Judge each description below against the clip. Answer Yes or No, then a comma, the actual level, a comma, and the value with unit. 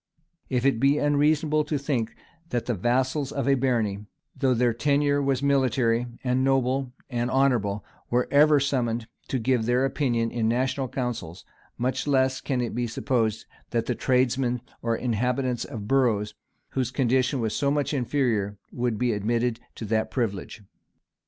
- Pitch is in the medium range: No, low, 125 Hz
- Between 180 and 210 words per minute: No, average, 160 wpm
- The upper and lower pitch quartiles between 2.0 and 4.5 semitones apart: Yes, average, 2.8 semitones